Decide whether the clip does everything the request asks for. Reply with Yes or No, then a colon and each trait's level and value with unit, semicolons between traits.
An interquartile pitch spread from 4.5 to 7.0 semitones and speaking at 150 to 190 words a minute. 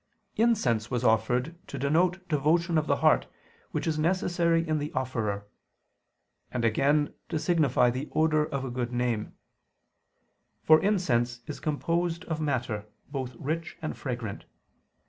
No: average, 5.1 semitones; average, 140 wpm